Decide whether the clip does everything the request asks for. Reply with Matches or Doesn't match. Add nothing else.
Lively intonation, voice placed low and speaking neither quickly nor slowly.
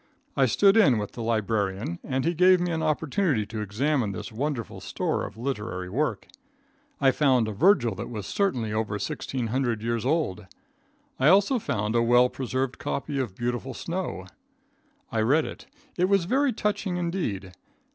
Matches